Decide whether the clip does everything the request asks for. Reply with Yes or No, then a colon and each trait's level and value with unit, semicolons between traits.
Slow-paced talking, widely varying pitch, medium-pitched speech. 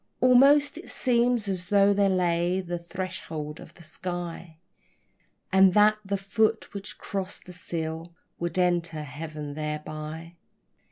No: slow, 130 wpm; average, 3.6 semitones; medium, 180 Hz